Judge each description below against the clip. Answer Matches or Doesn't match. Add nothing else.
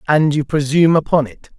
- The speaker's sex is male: Matches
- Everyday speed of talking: Matches